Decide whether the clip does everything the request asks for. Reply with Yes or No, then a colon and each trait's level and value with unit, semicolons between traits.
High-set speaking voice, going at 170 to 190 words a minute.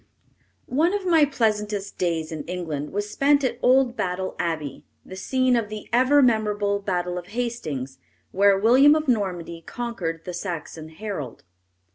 No: high, 205 Hz; average, 155 wpm